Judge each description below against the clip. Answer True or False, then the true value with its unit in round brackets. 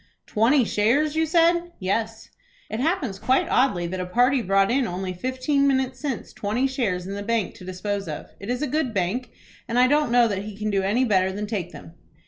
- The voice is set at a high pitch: True (225 Hz)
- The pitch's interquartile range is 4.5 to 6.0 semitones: True (5.2 semitones)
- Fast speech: True (215 wpm)